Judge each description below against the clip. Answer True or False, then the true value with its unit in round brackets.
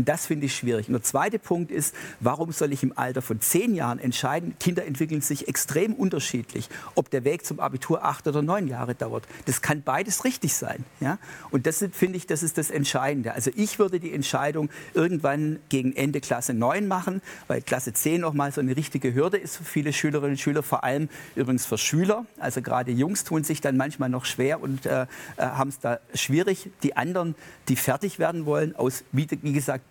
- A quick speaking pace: True (205 wpm)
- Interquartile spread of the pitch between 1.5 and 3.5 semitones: False (3.9 semitones)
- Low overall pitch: False (145 Hz)